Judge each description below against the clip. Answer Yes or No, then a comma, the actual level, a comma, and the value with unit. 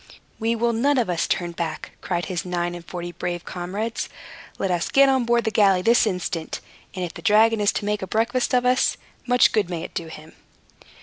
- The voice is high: Yes, high, 200 Hz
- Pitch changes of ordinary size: Yes, average, 4.9 semitones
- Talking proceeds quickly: Yes, fast, 220 wpm